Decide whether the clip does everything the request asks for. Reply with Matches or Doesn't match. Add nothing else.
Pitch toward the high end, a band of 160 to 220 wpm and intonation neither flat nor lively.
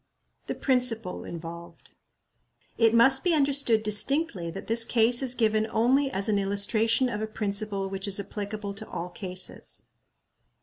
Doesn't match